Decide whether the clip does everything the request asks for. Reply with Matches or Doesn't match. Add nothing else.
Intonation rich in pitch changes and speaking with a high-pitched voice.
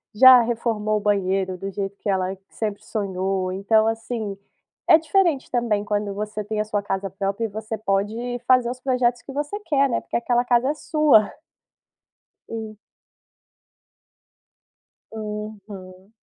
Doesn't match